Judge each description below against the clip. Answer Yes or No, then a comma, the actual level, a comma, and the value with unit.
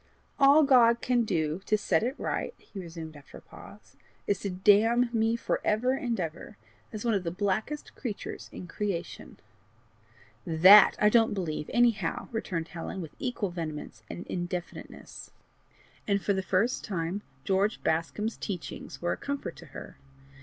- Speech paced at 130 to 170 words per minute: Yes, average, 160 wpm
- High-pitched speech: Yes, high, 200 Hz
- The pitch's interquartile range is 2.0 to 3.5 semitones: No, average, 5.0 semitones